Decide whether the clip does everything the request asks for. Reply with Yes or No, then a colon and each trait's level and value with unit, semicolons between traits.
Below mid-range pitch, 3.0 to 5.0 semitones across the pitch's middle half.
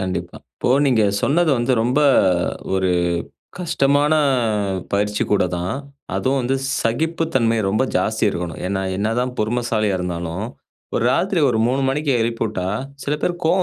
No: low, 120 Hz; wide, 5.6 semitones